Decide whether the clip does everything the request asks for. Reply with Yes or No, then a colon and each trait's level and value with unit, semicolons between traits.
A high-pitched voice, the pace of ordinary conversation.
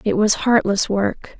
Yes: high, 210 Hz; average, 175 wpm